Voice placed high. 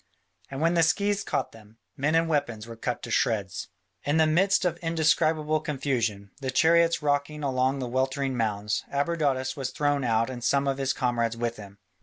No: low, 135 Hz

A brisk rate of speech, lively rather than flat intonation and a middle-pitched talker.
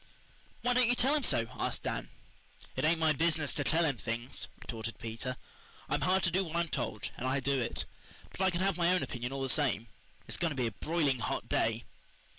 Yes: fast, 230 wpm; wide, 5.8 semitones; medium, 150 Hz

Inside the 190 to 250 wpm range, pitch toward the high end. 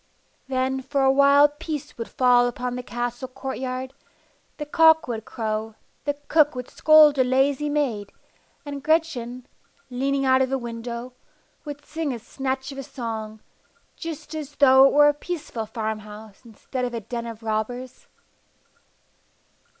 No: average, 155 wpm; very high, 260 Hz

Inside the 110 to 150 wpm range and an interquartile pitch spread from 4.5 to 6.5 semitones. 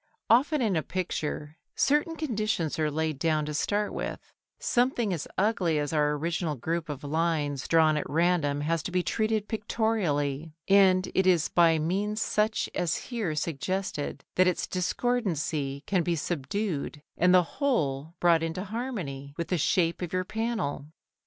No: average, 160 wpm; average, 5.3 semitones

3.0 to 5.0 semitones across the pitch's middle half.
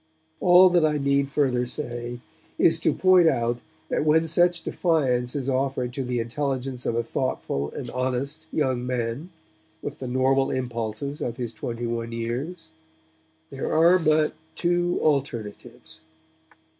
Yes: average, 4.2 semitones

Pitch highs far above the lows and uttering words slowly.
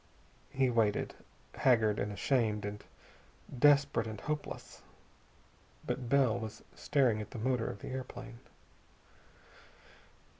No: average, 3.6 semitones; slow, 110 wpm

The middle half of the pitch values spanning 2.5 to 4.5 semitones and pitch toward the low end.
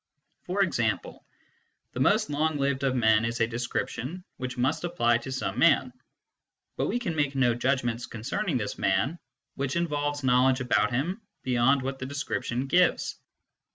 Yes: average, 3.4 semitones; low, 130 Hz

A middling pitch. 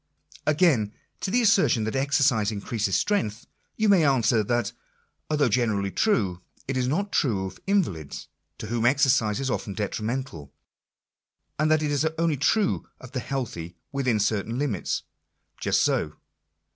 No: low, 125 Hz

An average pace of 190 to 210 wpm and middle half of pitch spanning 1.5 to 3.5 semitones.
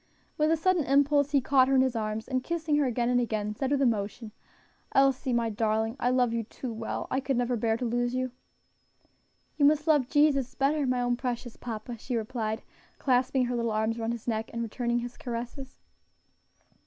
Yes: average, 200 wpm; average, 2.8 semitones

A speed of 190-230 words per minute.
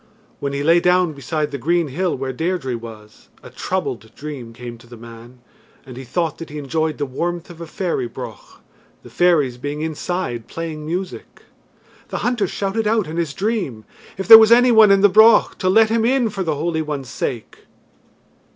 Yes: average, 195 wpm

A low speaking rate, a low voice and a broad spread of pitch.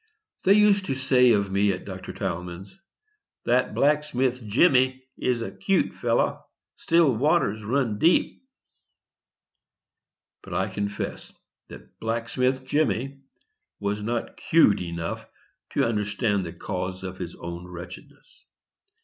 Yes: slow, 120 wpm; low, 115 Hz; wide, 5.7 semitones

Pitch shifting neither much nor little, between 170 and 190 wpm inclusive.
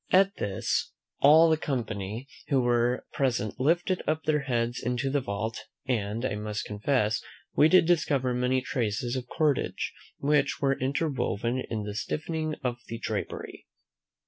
No: average, 4.4 semitones; average, 145 wpm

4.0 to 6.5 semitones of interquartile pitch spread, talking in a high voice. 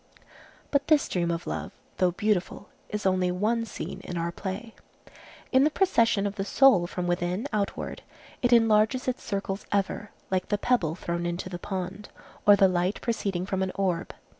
No: average, 3.6 semitones; high, 195 Hz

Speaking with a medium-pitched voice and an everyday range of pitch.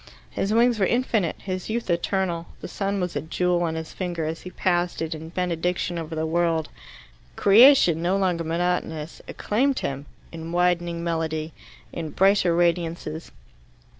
No: medium, 175 Hz; narrow, 2.3 semitones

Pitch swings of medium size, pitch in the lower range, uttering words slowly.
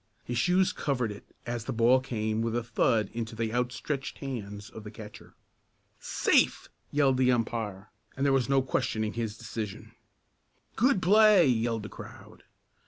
No: average, 3.4 semitones; low, 120 Hz; average, 160 wpm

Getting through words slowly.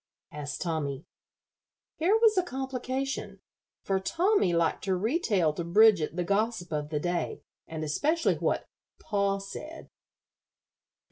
Yes: slow, 125 wpm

